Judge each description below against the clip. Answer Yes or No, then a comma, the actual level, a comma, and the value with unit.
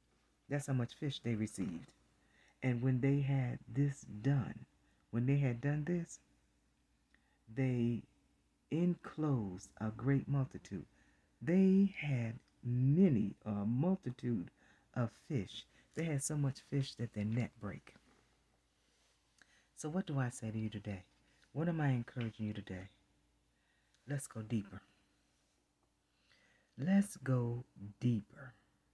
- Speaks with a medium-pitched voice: No, low, 120 Hz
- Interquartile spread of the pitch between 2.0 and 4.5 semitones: No, average, 5.2 semitones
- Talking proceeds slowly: Yes, slow, 120 wpm